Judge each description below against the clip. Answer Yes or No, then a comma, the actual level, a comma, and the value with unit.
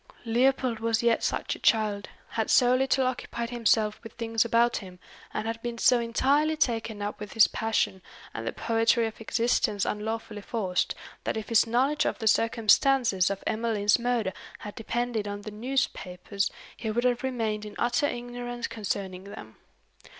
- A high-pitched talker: Yes, high, 225 Hz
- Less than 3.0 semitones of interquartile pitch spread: Yes, narrow, 2.4 semitones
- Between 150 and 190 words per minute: Yes, average, 165 wpm